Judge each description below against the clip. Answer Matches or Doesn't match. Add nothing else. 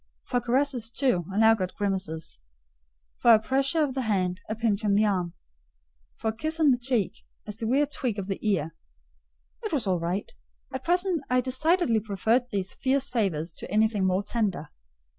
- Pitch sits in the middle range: Doesn't match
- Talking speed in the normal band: Matches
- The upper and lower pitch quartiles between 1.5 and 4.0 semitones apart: Doesn't match